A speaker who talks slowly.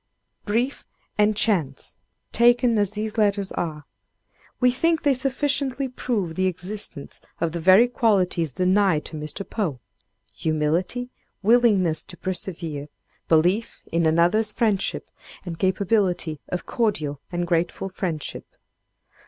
Yes: slow, 120 wpm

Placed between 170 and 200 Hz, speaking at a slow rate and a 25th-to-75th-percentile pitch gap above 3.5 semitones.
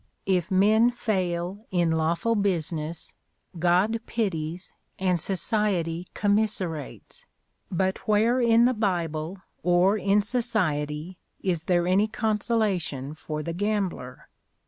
Yes: medium, 185 Hz; slow, 105 wpm; average, 4.1 semitones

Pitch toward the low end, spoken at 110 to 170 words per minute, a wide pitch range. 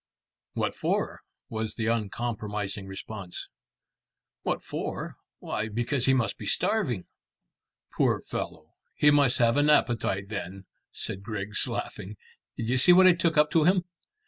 Yes: low, 115 Hz; average, 145 wpm; wide, 6.0 semitones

